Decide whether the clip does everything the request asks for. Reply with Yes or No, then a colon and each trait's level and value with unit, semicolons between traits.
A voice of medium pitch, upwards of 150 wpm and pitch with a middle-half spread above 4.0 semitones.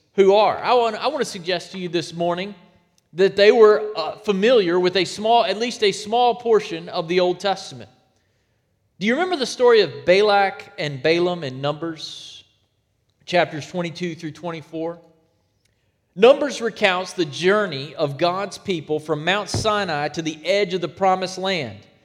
Yes: medium, 180 Hz; average, 165 wpm; average, 5.1 semitones